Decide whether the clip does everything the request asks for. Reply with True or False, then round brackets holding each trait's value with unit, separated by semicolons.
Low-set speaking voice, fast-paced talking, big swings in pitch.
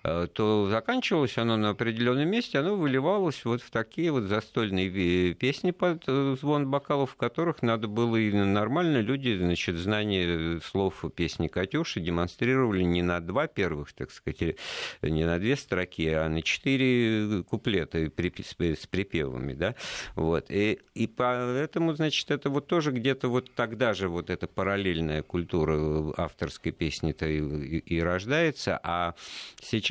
False (110 Hz; 140 wpm; 7.5 semitones)